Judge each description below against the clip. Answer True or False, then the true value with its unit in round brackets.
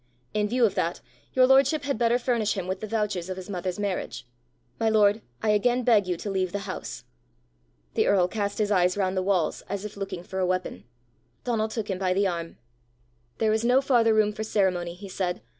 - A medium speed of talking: False (215 wpm)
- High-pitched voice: True (205 Hz)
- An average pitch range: True (3.1 semitones)